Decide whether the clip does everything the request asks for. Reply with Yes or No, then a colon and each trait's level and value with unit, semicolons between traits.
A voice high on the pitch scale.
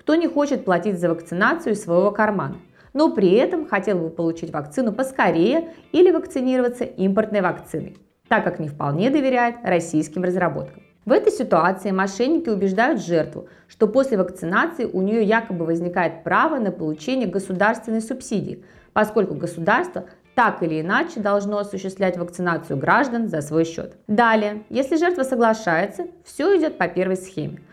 Yes: high, 205 Hz